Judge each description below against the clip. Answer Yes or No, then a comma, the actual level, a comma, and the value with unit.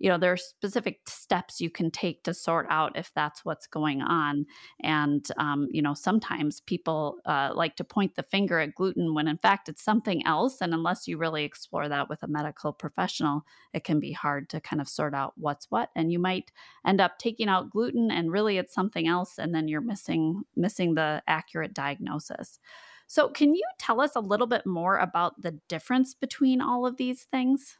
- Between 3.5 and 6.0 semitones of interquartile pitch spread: Yes, wide, 5.5 semitones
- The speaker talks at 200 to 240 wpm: Yes, fast, 205 wpm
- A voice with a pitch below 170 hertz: No, medium, 175 Hz